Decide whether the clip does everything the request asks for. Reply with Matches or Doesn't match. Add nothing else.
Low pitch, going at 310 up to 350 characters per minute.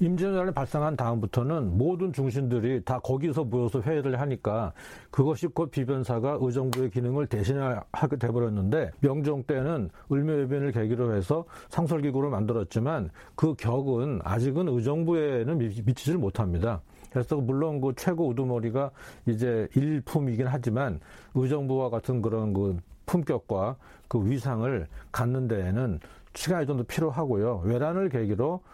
Matches